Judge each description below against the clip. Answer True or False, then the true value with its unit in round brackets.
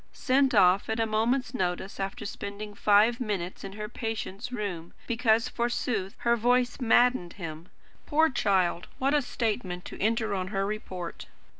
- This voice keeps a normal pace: True (155 wpm)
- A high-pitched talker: True (215 Hz)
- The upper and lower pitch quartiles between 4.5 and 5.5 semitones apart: False (3.9 semitones)